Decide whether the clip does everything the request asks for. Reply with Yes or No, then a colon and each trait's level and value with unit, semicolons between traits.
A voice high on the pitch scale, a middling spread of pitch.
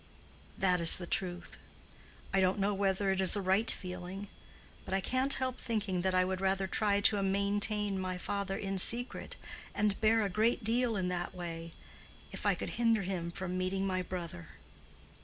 No: high, 195 Hz; narrow, 2.1 semitones